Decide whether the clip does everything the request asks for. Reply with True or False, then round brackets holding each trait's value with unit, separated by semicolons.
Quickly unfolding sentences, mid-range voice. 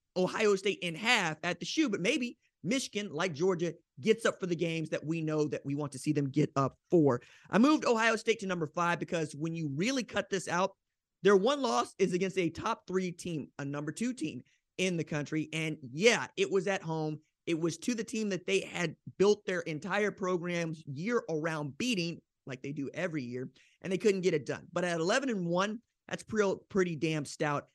True (215 wpm; 175 Hz)